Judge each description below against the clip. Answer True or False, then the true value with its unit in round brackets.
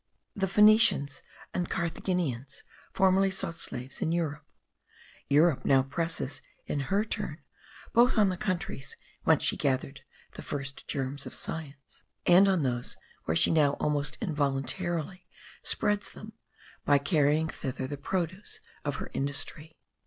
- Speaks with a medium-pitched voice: True (155 Hz)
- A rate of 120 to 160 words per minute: True (135 wpm)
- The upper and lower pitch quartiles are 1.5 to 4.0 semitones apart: False (4.9 semitones)